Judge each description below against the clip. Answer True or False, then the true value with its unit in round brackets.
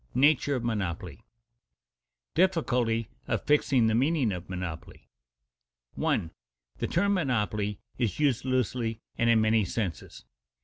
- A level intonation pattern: False (4.7 semitones)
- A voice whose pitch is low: True (115 Hz)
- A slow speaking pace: True (125 wpm)